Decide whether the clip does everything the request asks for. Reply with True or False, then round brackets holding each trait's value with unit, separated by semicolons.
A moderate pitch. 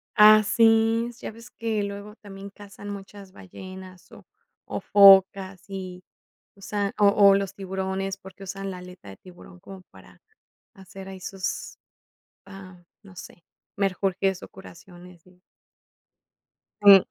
False (195 Hz)